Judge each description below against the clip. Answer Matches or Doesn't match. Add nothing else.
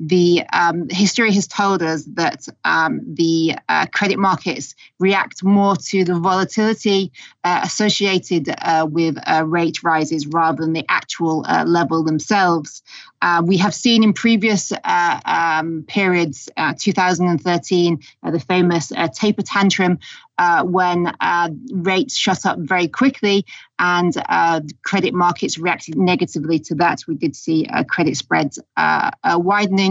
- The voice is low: Doesn't match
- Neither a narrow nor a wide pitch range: Matches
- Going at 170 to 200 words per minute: Doesn't match